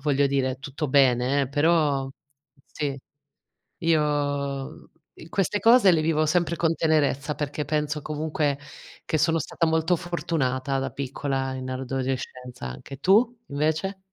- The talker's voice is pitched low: No, medium, 145 Hz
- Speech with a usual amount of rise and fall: Yes, average, 3.1 semitones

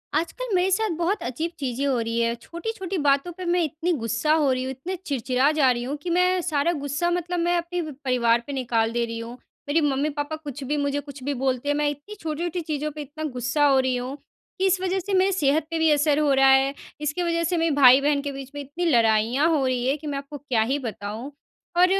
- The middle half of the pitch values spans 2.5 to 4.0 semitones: No, average, 4.4 semitones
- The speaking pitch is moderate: No, very high, 290 Hz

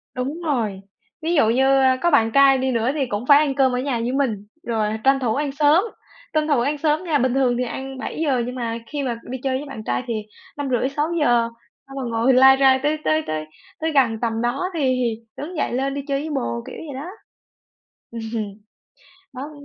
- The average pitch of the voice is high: Yes, very high, 265 Hz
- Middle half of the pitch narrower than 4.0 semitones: Yes, average, 3.4 semitones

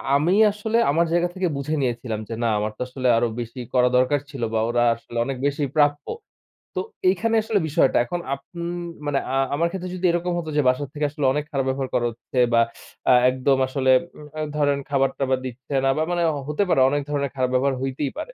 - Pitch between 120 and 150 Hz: Yes, medium, 140 Hz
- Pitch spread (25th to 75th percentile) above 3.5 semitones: No, average, 3.2 semitones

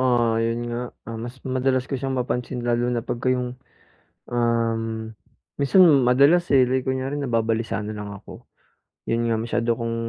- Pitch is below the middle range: Yes, low, 120 Hz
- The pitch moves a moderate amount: No, narrow, 2.1 semitones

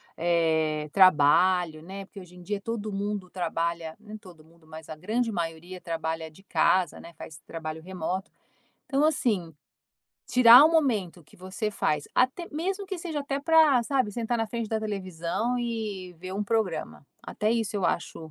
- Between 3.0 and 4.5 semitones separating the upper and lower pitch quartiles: No, wide, 5.5 semitones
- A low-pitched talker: No, high, 190 Hz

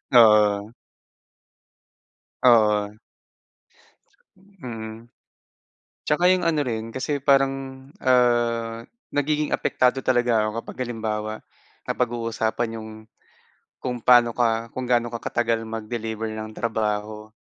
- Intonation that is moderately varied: No, narrow, 2.3 semitones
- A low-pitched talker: Yes, low, 115 Hz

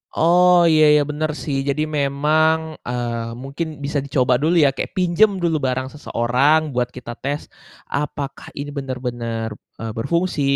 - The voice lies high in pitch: No, medium, 140 Hz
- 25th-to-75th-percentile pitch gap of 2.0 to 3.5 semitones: No, average, 4.0 semitones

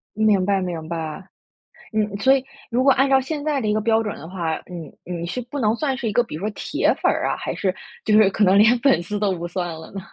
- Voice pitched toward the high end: Yes, high, 210 Hz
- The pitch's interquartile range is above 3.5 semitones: Yes, average, 5.0 semitones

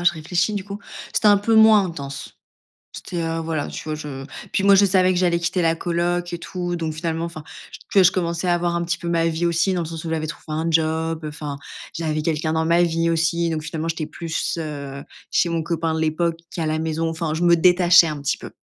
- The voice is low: No, medium, 165 Hz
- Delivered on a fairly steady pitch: Yes, narrow, 1.6 semitones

